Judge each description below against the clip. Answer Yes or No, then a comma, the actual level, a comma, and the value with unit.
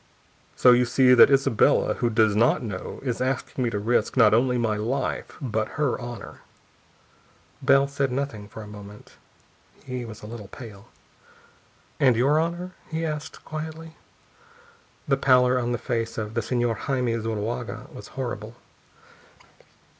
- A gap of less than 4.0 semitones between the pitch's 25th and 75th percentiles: Yes, average, 3.3 semitones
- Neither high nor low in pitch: No, low, 120 Hz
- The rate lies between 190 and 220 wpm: No, average, 150 wpm